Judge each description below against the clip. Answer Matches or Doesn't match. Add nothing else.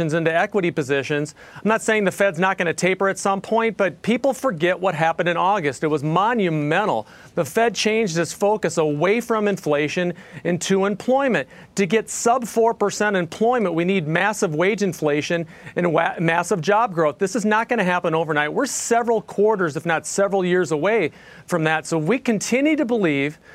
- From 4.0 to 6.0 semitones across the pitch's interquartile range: Matches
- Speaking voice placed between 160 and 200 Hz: Matches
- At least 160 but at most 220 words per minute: Matches